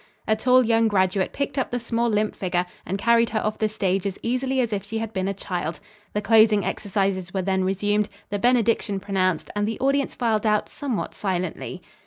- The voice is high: Yes, high, 210 Hz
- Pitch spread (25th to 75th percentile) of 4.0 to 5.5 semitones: No, average, 3.1 semitones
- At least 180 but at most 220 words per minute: Yes, fast, 205 wpm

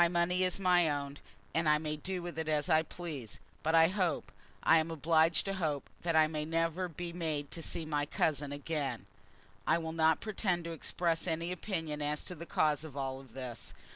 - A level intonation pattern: Yes, narrow, 2.3 semitones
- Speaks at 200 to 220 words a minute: Yes, fast, 205 wpm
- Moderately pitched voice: Yes, medium, 160 Hz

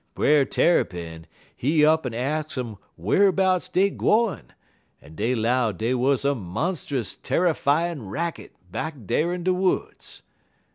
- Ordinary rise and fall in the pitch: No, wide, 7.1 semitones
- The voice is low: No, medium, 145 Hz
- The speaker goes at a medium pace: No, slow, 130 wpm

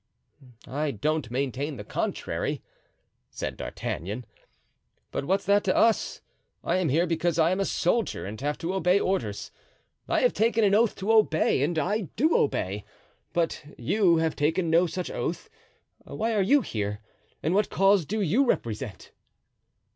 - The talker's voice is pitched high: No, medium, 170 Hz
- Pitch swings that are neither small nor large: No, wide, 5.9 semitones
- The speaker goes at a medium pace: Yes, average, 160 wpm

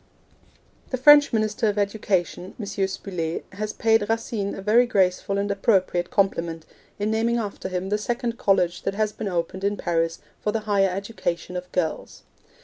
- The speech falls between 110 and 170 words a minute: Yes, average, 165 wpm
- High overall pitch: Yes, high, 200 Hz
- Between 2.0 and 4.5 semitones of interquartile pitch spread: Yes, average, 3.1 semitones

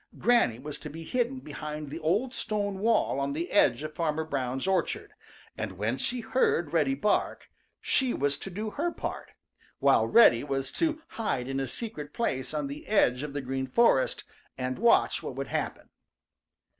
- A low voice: No, medium, 155 Hz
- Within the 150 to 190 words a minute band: Yes, average, 180 wpm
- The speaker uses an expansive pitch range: Yes, wide, 8.3 semitones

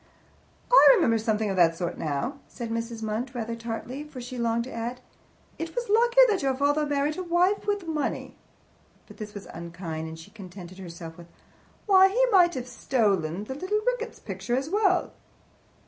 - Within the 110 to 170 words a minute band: No, average, 180 wpm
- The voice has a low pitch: No, high, 245 Hz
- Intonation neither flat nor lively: No, wide, 8.9 semitones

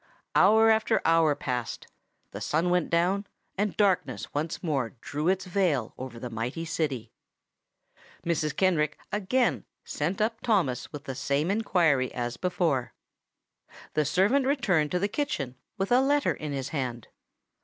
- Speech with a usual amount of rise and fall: No, wide, 6.1 semitones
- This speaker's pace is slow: No, average, 145 wpm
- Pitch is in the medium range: Yes, medium, 165 Hz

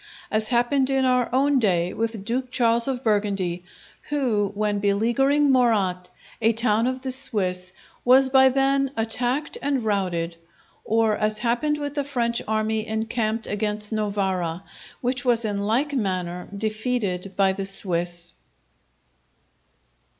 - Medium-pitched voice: No, high, 220 Hz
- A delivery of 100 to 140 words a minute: Yes, slow, 135 wpm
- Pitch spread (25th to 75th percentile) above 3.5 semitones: Yes, average, 4.2 semitones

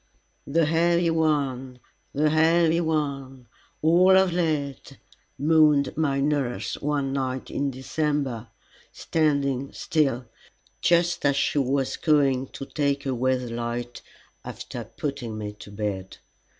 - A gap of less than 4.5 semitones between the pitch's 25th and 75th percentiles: Yes, average, 3.3 semitones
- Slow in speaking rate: Yes, slow, 120 wpm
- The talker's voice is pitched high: No, medium, 140 Hz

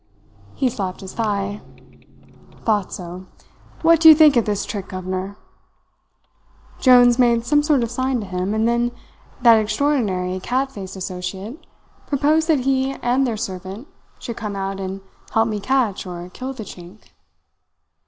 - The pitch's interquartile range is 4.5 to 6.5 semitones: Yes, average, 5.3 semitones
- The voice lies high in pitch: Yes, high, 220 Hz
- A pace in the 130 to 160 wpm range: Yes, average, 155 wpm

